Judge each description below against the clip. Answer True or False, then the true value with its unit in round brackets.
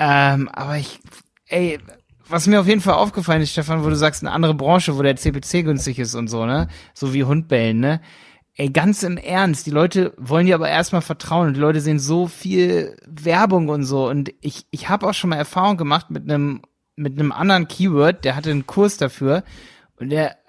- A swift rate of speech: True (210 wpm)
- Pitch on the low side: False (155 Hz)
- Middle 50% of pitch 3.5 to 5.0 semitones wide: True (3.9 semitones)